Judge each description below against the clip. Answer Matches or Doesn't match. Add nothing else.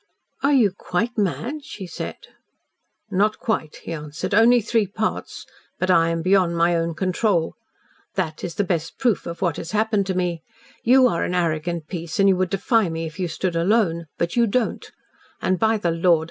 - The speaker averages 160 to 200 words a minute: Matches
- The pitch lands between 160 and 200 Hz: Matches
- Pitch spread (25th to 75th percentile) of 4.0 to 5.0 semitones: Matches